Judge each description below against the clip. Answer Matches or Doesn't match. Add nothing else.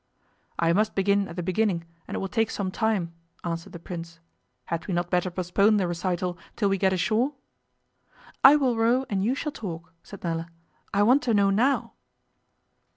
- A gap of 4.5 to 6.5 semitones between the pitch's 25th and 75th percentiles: Doesn't match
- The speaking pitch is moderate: Doesn't match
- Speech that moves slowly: Doesn't match